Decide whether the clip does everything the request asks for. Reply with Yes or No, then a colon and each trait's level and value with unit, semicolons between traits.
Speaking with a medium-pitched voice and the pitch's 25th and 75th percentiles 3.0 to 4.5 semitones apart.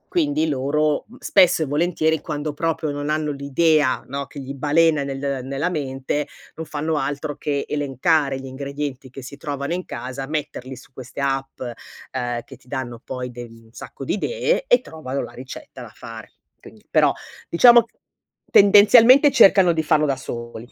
Yes: medium, 145 Hz; average, 3.3 semitones